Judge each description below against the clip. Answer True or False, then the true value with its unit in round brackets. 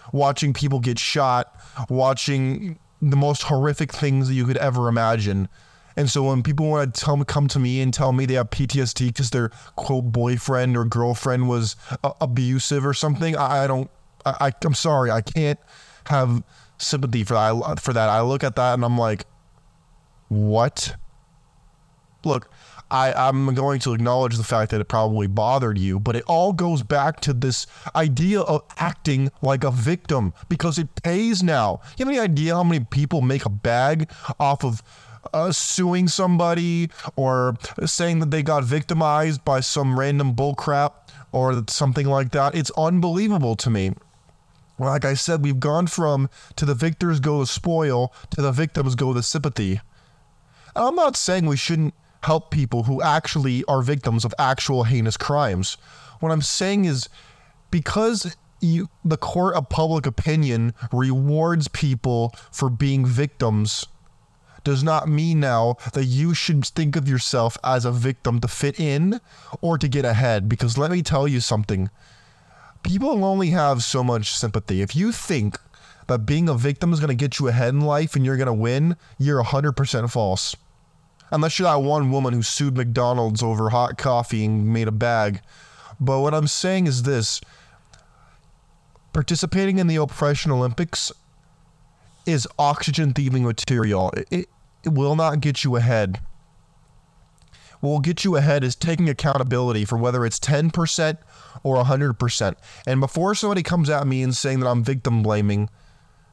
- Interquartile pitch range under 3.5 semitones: False (4.1 semitones)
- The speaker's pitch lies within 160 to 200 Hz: False (140 Hz)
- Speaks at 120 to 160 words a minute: False (170 wpm)